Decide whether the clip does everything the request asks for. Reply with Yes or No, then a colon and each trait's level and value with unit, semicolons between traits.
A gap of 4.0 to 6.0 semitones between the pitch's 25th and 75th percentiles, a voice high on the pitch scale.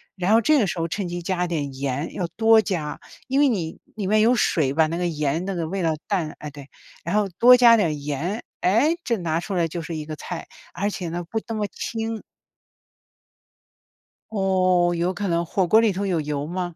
No: average, 4.5 semitones; medium, 180 Hz